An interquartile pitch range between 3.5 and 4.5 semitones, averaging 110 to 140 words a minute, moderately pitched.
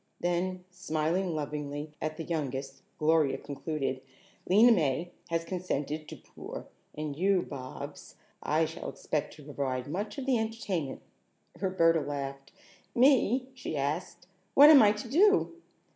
No: average, 5.1 semitones; slow, 135 wpm; medium, 165 Hz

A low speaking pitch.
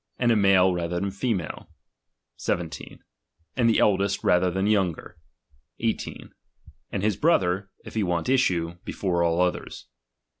Yes: very low, 95 Hz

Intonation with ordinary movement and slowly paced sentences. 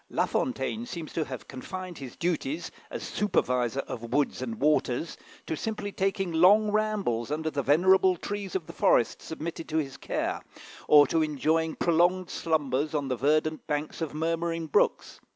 No: average, 4.1 semitones; average, 165 wpm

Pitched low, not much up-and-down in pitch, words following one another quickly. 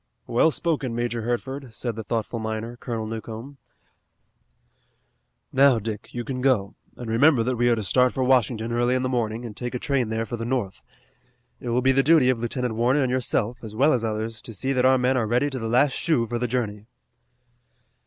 Yes: low, 120 Hz; narrow, 2.3 semitones; fast, 215 wpm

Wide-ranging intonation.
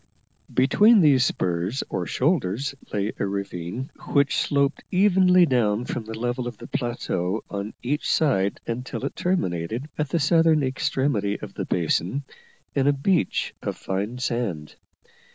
Yes: wide, 6.1 semitones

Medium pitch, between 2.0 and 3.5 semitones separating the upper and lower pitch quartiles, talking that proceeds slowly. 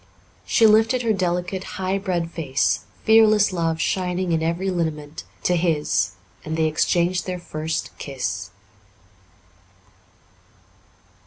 Yes: medium, 175 Hz; average, 2.9 semitones; slow, 110 wpm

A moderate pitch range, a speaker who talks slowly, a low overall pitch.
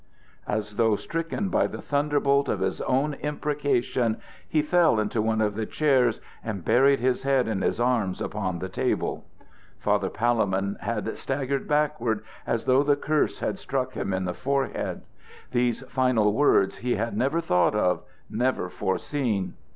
No: average, 4.8 semitones; average, 160 wpm; low, 120 Hz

